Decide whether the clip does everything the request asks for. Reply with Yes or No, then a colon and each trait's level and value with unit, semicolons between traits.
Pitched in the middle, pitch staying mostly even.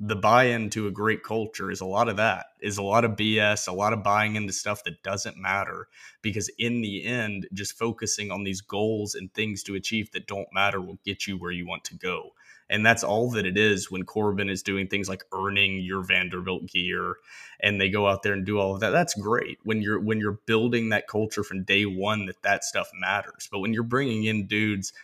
No: low, 105 Hz; narrow, 2.0 semitones